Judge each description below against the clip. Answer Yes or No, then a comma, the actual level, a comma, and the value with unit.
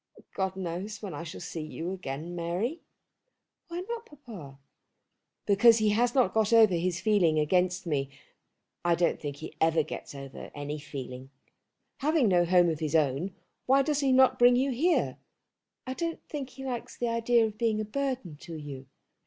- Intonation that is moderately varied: No, wide, 7.4 semitones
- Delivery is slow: No, average, 175 wpm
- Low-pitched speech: No, high, 190 Hz